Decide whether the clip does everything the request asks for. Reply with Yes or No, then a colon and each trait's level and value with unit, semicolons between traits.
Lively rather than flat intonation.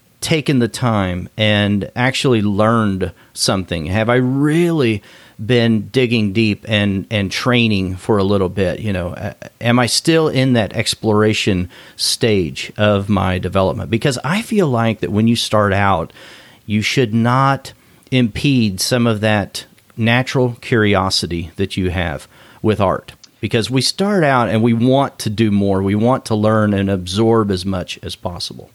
No: average, 3.8 semitones